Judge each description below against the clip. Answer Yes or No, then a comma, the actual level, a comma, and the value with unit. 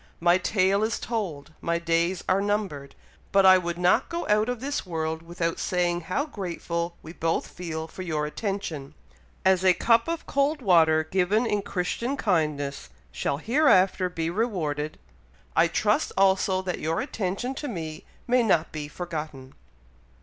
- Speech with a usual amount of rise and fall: Yes, average, 4.1 semitones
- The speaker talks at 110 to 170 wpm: Yes, average, 155 wpm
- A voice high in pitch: No, medium, 180 Hz